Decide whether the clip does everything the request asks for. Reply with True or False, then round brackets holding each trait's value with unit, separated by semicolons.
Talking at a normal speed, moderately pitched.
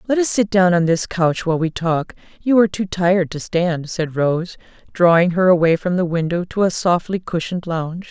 False (215 wpm; 175 Hz)